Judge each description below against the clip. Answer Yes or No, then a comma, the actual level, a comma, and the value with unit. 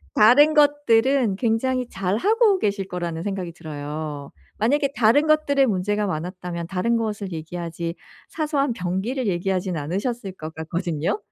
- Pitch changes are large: Yes, wide, 6.8 semitones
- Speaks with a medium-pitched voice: No, high, 200 Hz